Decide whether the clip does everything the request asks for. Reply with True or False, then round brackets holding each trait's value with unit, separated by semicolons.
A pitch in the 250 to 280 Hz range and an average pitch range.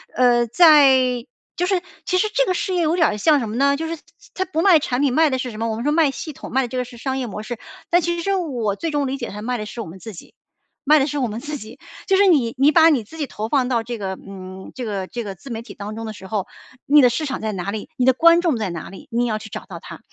False (255 Hz; 5.9 semitones)